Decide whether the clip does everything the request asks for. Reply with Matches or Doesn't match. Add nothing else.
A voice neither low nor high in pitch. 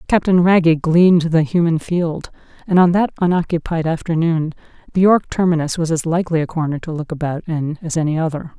Matches